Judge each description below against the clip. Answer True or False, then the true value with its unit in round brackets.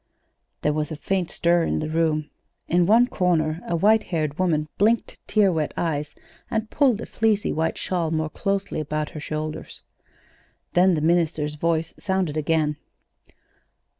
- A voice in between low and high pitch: True (165 Hz)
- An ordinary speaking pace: True (155 wpm)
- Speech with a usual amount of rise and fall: True (3.6 semitones)